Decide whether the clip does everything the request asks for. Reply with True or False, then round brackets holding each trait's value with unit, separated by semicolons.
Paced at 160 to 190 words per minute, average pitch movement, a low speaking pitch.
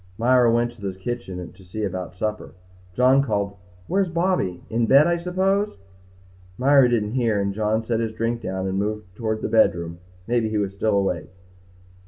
True (180 wpm; 3.9 semitones; 110 Hz)